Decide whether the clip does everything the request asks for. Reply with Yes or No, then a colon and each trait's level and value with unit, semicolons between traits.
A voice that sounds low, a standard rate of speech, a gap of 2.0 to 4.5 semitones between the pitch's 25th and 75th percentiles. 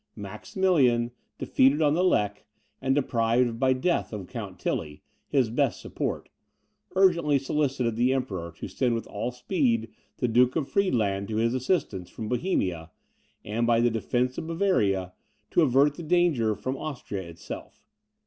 No: low, 125 Hz; average, 150 wpm; average, 5.1 semitones